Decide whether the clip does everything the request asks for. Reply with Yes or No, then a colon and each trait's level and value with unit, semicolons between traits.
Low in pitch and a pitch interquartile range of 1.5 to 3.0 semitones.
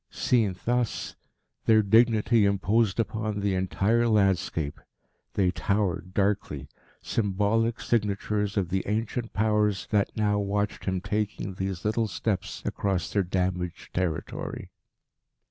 Yes: low, 100 Hz; narrow, 2.4 semitones